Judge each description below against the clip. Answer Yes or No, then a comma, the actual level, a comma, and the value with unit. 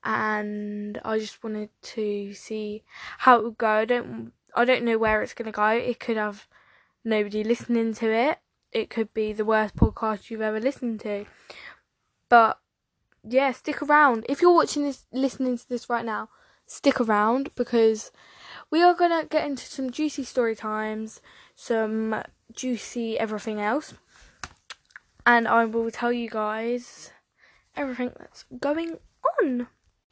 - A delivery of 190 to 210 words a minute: No, average, 150 wpm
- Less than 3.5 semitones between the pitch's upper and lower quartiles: Yes, average, 3.1 semitones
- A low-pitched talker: No, high, 230 Hz